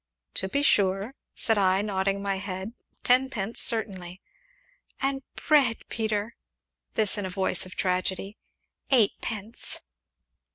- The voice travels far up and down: No, average, 3.1 semitones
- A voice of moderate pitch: No, high, 200 Hz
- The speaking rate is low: Yes, slow, 120 wpm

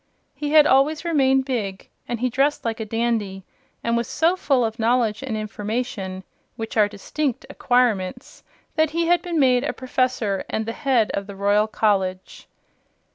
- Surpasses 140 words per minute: Yes, average, 170 wpm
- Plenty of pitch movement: No, average, 4.3 semitones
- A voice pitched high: Yes, high, 235 Hz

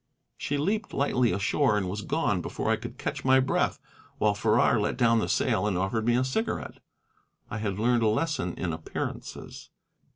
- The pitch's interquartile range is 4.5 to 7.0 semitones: No, average, 3.9 semitones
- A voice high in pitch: No, low, 110 Hz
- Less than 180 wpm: No, average, 185 wpm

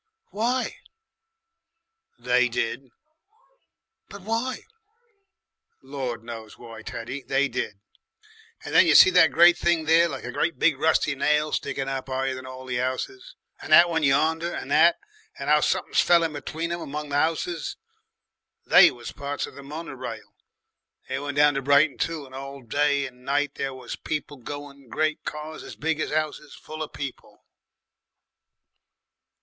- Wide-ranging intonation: No, average, 3.5 semitones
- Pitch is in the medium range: Yes, medium, 145 Hz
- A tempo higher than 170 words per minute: No, average, 160 wpm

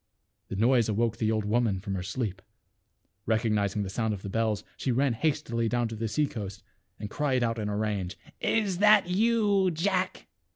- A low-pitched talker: Yes, low, 115 Hz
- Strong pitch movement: Yes, wide, 6.1 semitones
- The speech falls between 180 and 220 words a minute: Yes, average, 195 wpm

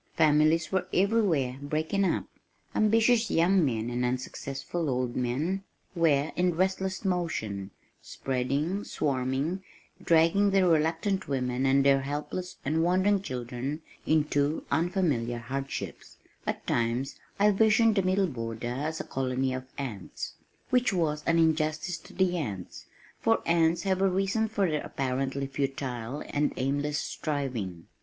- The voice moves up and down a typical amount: No, wide, 5.7 semitones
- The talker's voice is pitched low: No, medium, 150 Hz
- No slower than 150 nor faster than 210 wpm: No, slow, 135 wpm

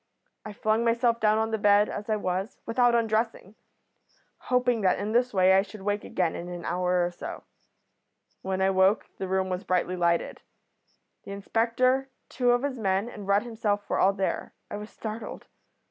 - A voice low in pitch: No, high, 205 Hz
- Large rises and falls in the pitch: No, average, 3.3 semitones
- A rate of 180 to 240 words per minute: Yes, average, 185 wpm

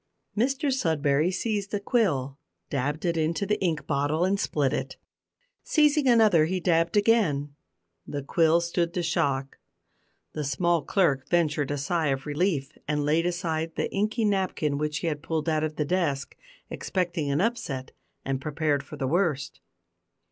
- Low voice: No, medium, 160 Hz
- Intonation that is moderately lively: Yes, average, 4.3 semitones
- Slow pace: No, average, 160 wpm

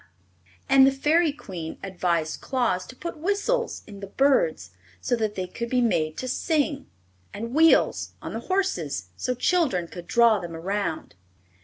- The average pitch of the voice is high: Yes, high, 230 Hz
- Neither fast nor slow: Yes, average, 155 wpm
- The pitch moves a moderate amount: No, wide, 8.2 semitones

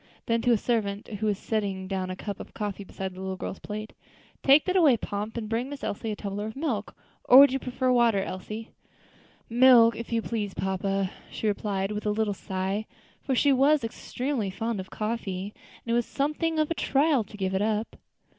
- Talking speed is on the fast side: Yes, fast, 210 wpm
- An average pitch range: Yes, average, 3.7 semitones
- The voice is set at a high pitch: Yes, high, 220 Hz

